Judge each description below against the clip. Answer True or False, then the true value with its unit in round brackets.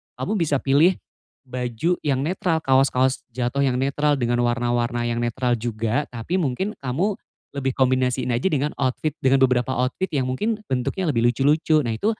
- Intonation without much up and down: False (3.5 semitones)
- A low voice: True (130 Hz)